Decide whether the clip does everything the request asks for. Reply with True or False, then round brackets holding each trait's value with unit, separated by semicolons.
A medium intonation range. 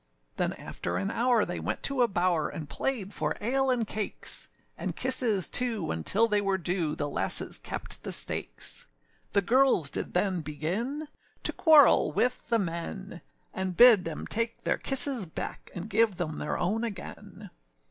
False (5.7 semitones)